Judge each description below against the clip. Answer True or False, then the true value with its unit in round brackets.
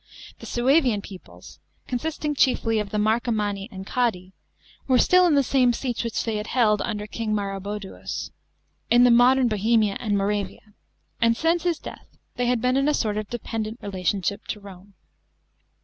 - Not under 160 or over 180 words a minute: True (165 wpm)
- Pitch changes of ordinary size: True (3.3 semitones)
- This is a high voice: True (225 Hz)